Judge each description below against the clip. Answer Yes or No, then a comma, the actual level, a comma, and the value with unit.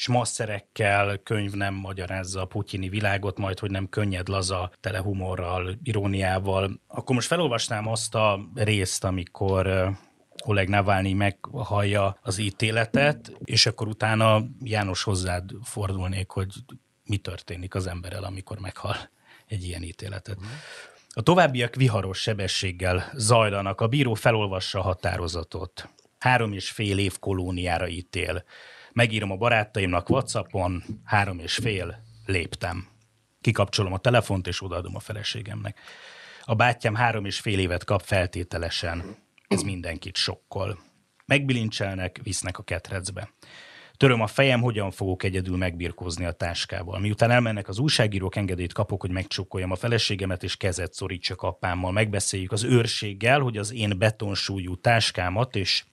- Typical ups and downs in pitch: Yes, average, 3.0 semitones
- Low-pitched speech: Yes, low, 100 Hz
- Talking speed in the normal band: Yes, average, 130 wpm